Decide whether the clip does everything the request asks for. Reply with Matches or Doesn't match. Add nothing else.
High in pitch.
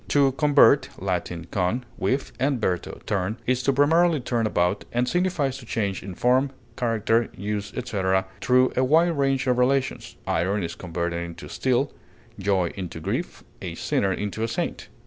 Doesn't match